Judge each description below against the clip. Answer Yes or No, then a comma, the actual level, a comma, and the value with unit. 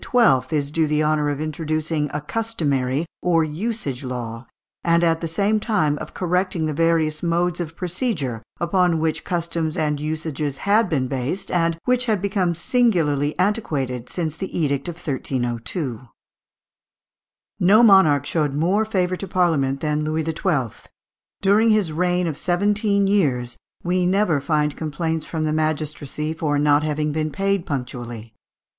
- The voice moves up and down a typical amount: Yes, average, 3.7 semitones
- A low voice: No, medium, 160 Hz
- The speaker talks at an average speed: Yes, average, 150 wpm